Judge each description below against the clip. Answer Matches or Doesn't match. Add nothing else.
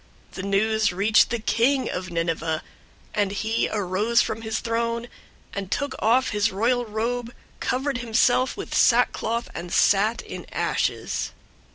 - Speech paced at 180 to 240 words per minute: Doesn't match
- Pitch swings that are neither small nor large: Matches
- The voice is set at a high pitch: Matches